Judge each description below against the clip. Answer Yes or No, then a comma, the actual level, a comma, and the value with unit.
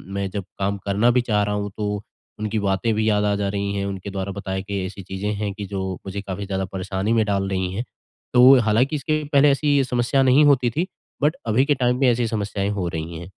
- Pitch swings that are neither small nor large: Yes, average, 3.8 semitones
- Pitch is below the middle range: Yes, low, 105 Hz